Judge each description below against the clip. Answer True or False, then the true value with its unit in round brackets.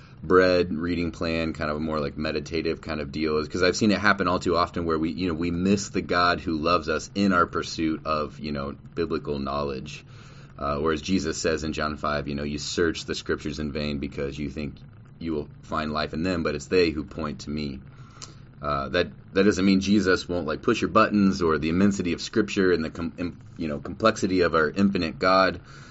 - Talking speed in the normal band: False (225 wpm)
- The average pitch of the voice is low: True (80 Hz)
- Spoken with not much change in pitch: False (3.7 semitones)